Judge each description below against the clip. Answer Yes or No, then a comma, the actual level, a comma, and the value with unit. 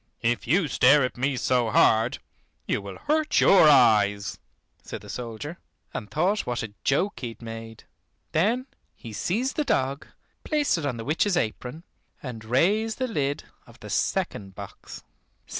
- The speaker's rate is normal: Yes, average, 160 wpm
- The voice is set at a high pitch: No, low, 135 Hz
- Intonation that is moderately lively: No, wide, 8.2 semitones